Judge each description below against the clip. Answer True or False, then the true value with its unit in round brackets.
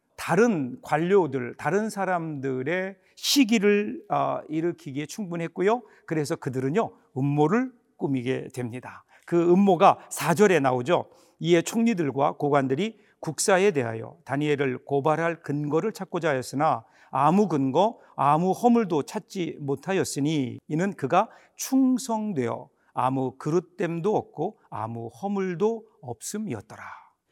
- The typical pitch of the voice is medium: True (165 Hz)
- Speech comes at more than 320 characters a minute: False (275 characters per minute)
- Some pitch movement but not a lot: False (6.1 semitones)